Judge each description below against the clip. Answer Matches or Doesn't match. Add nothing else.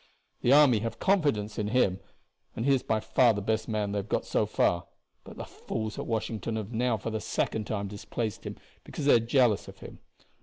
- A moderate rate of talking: Doesn't match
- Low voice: Matches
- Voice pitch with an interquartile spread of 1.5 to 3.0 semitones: Matches